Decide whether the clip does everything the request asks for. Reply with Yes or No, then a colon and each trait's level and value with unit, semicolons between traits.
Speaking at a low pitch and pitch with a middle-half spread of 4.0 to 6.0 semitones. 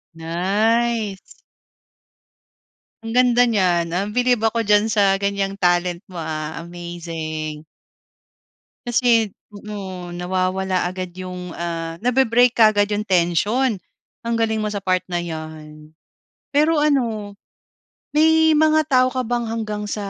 No: high, 205 Hz; average, 4.8 semitones